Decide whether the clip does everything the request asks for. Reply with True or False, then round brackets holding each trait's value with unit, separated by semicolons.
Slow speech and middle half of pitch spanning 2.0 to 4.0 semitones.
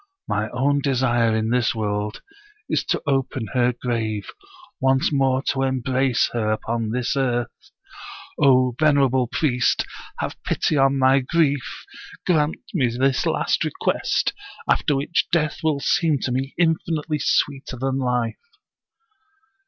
True (130 wpm; 2.8 semitones)